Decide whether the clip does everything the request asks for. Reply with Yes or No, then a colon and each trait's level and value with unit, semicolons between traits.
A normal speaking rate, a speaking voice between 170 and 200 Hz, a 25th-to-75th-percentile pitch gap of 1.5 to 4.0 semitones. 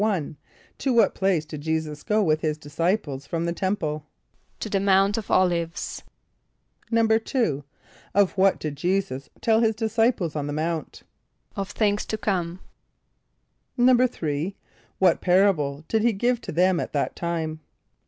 No: average, 145 wpm; medium, 185 Hz; average, 5.2 semitones